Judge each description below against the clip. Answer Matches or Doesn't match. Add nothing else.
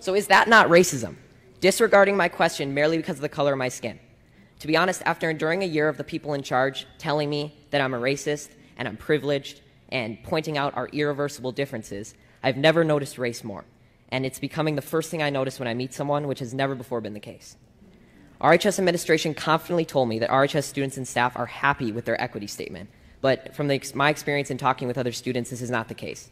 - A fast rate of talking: Matches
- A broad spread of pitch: Doesn't match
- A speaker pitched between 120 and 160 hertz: Matches